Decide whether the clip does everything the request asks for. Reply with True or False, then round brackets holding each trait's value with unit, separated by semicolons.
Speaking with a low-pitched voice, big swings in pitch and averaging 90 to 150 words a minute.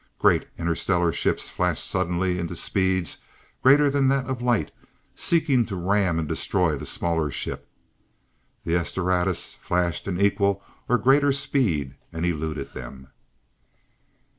True (90 Hz; 6.3 semitones; 135 wpm)